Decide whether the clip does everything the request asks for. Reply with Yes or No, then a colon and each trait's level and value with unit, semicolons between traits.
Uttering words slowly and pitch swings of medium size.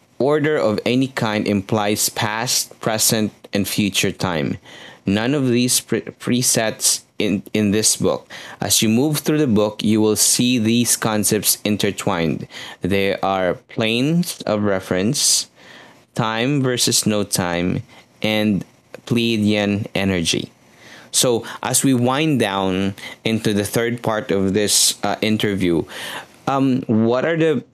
Yes: slow, 130 wpm; average, 3.3 semitones